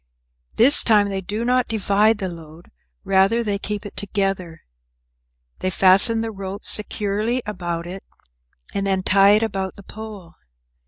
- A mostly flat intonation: Yes, narrow, 2.3 semitones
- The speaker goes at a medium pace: Yes, average, 150 wpm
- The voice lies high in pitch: Yes, high, 200 Hz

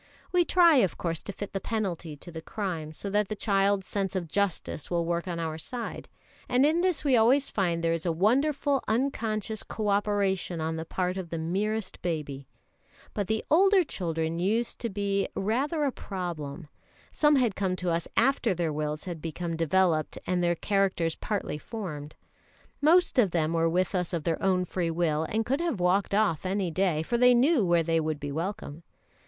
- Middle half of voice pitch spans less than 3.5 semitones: No, average, 4.8 semitones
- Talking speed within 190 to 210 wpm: Yes, average, 195 wpm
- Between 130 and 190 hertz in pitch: Yes, medium, 185 Hz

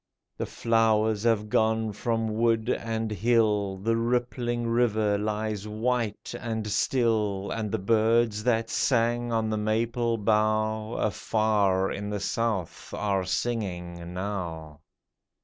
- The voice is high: No, low, 110 Hz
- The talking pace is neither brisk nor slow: No, slow, 120 wpm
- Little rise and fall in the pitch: Yes, narrow, 1.9 semitones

